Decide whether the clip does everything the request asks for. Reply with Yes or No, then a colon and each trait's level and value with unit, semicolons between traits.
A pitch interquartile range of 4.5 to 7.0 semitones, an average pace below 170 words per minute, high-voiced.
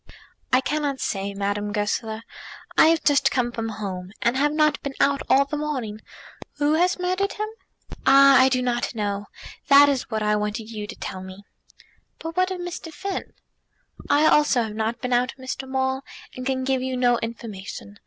No: average, 5.1 semitones; average, 185 wpm; very high, 255 Hz